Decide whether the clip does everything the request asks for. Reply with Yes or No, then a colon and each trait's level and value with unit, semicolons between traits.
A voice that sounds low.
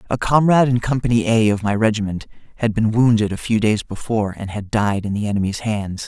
Yes: low, 110 Hz